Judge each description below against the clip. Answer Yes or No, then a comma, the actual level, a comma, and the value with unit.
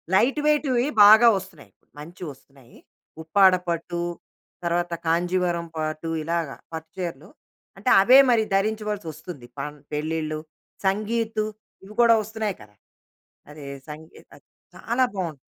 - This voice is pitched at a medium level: Yes, medium, 175 Hz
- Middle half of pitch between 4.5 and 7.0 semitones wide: Yes, average, 5.2 semitones